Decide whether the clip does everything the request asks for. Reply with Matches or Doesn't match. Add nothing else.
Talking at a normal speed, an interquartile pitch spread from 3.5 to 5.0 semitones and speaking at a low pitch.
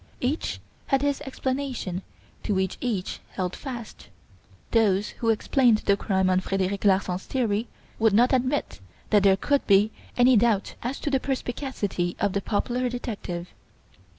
Doesn't match